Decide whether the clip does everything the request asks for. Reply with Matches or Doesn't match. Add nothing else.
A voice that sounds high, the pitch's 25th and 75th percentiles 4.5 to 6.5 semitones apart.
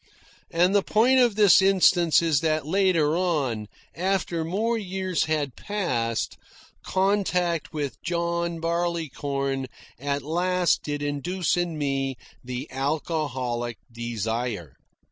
Doesn't match